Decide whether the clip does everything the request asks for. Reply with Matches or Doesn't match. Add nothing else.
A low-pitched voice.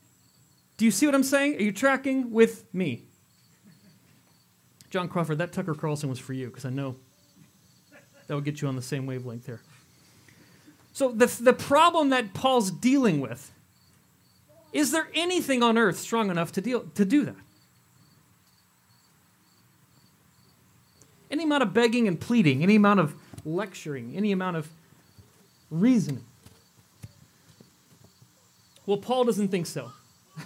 Doesn't match